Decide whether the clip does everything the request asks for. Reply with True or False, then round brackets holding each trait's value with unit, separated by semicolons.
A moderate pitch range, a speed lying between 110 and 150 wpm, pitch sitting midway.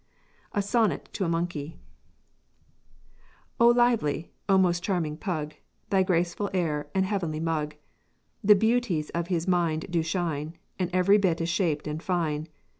True (3.4 semitones; 140 wpm; 170 Hz)